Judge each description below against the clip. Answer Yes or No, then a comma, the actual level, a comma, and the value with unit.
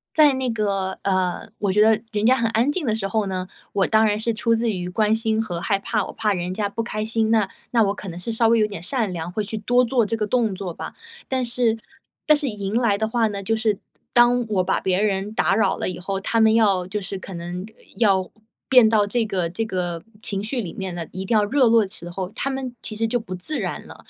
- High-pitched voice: Yes, high, 215 Hz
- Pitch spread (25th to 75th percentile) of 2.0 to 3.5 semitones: Yes, average, 3.2 semitones